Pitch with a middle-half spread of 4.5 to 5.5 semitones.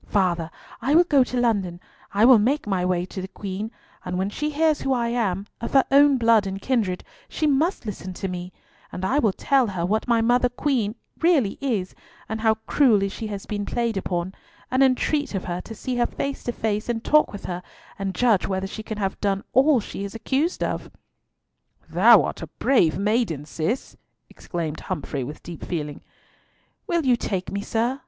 Yes: average, 5.2 semitones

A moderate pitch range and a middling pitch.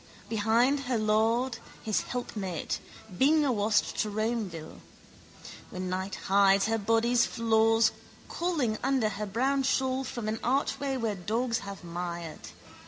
No: average, 3.7 semitones; high, 225 Hz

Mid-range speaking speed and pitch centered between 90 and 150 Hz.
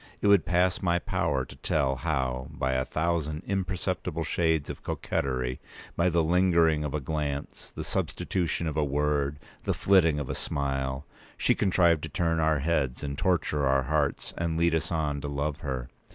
No: average, 170 wpm; very low, 75 Hz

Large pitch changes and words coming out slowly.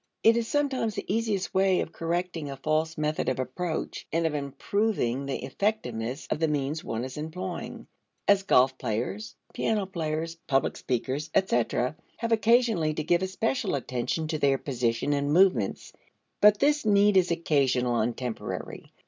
No: wide, 6.7 semitones; average, 155 wpm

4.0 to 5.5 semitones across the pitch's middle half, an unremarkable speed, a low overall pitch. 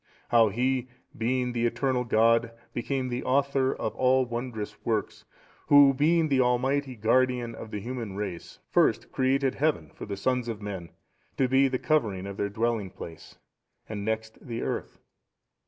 No: average, 3.1 semitones; average, 160 wpm; low, 120 Hz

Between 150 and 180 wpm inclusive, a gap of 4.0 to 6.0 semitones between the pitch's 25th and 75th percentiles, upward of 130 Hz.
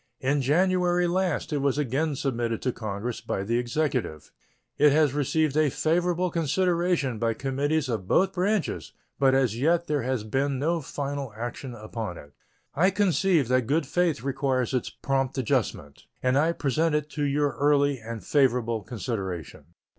Yes: average, 160 wpm; average, 4.6 semitones; medium, 140 Hz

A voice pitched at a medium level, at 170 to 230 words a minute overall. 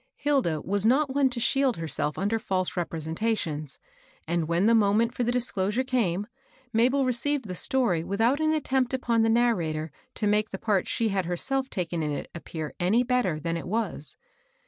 No: high, 215 Hz; average, 185 wpm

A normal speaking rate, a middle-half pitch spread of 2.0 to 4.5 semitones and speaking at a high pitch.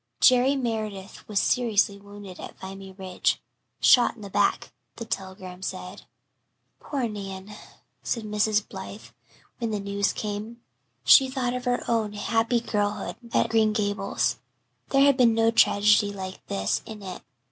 Yes: average, 150 wpm; narrow, 2.6 semitones; high, 210 Hz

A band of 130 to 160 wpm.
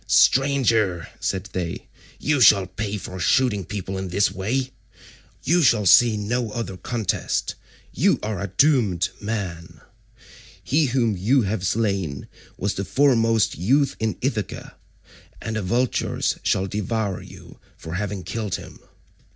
Yes: slow, 135 wpm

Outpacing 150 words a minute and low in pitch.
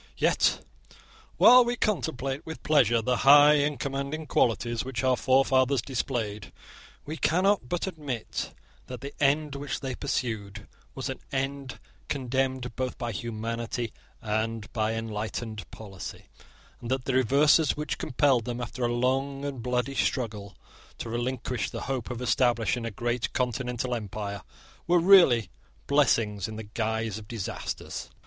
No: average, 140 wpm; low, 125 Hz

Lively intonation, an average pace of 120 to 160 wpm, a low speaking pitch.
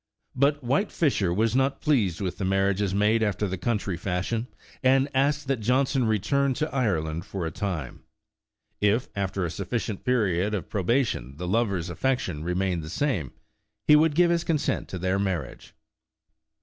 No: wide, 6.3 semitones; average, 175 wpm; low, 105 Hz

